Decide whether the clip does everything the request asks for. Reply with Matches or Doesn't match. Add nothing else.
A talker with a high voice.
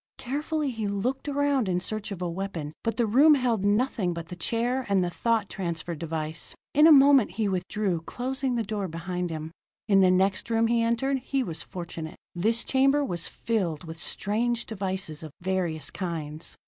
Matches